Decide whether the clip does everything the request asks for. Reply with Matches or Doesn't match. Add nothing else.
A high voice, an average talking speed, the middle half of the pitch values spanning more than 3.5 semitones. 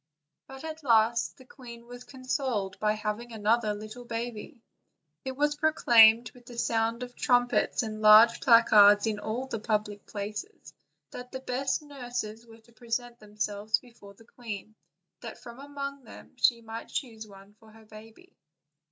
Doesn't match